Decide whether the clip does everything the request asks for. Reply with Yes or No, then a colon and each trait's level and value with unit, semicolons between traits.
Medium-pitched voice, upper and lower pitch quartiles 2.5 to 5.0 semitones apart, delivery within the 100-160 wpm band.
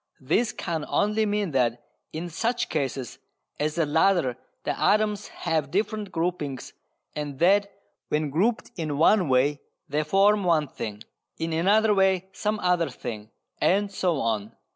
No: medium, 170 Hz; wide, 5.6 semitones; average, 145 wpm